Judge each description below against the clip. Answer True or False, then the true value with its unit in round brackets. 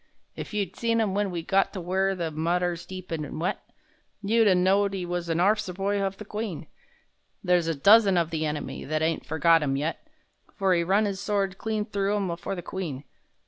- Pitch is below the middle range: False (185 Hz)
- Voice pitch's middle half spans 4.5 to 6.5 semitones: False (3.2 semitones)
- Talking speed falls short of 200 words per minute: False (205 wpm)